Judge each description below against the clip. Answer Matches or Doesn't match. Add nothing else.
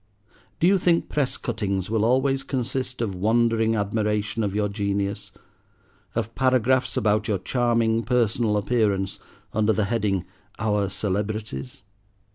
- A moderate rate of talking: Doesn't match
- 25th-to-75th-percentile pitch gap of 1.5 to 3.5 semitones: Matches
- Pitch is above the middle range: Doesn't match